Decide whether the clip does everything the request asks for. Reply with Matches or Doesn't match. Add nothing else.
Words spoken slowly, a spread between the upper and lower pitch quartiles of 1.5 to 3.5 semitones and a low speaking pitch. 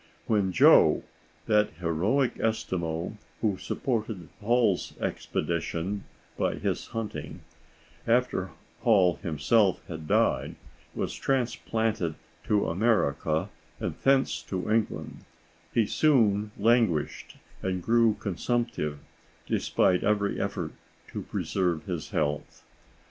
Doesn't match